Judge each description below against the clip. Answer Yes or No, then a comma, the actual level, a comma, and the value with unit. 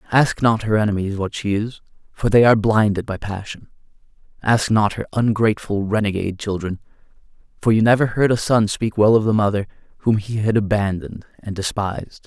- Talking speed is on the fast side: No, average, 175 wpm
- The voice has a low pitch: Yes, low, 105 Hz